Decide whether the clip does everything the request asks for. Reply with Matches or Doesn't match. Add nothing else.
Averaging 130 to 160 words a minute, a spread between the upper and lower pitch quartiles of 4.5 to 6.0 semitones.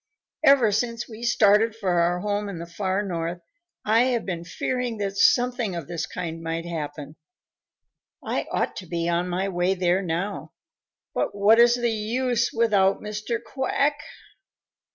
Matches